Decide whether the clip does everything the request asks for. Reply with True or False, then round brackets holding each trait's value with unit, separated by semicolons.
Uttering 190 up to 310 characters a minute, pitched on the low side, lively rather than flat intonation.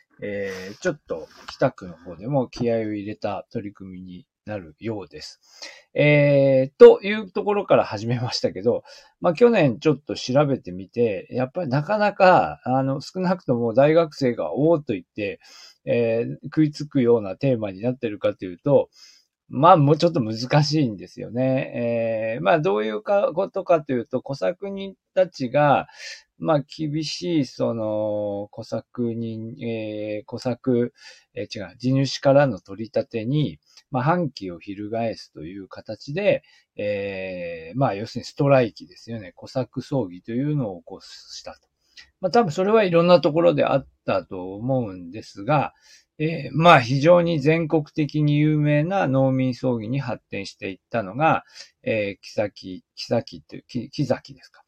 True (305 characters per minute; 130 Hz; 5.9 semitones)